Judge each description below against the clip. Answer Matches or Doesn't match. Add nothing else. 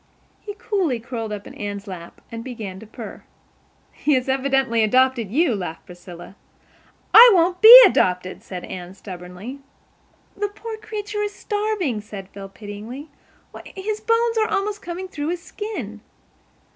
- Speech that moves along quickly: Doesn't match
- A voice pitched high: Matches